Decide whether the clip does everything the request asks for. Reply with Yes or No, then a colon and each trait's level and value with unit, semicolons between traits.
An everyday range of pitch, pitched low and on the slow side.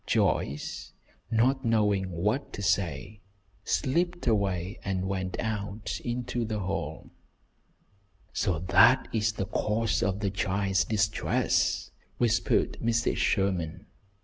Yes: average, 3.1 semitones; low, 100 Hz; slow, 110 wpm